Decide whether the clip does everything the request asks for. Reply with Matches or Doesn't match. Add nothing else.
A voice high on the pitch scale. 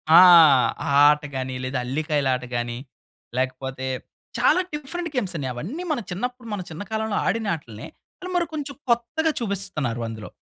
Doesn't match